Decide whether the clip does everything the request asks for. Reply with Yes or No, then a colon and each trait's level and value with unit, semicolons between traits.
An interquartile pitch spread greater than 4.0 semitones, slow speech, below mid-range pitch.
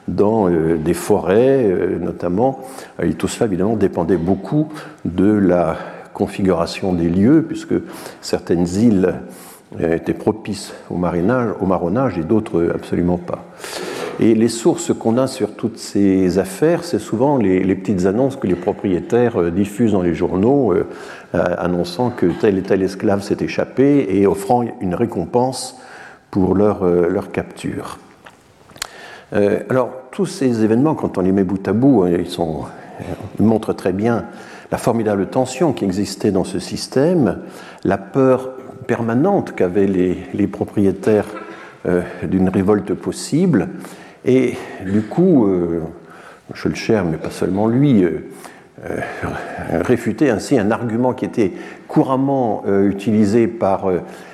Yes: average, 5.0 semitones; slow, 140 wpm; low, 105 Hz